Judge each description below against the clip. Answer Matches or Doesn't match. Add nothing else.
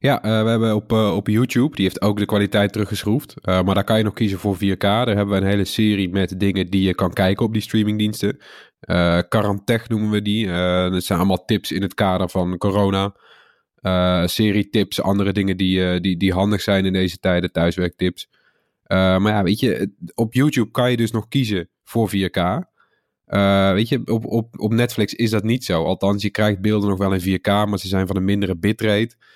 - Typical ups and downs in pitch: Doesn't match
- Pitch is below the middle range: Matches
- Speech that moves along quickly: Matches